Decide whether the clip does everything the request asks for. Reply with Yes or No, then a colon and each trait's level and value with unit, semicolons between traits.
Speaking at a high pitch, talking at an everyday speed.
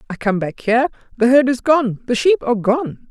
No: high, 245 Hz; fast, 230 wpm